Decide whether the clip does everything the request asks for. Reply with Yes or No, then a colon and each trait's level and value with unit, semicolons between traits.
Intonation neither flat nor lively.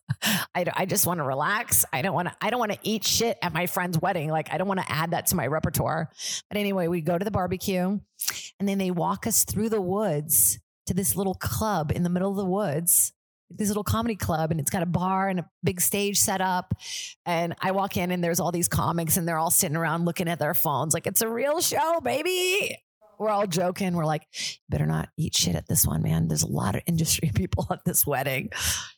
Yes: average, 3.5 semitones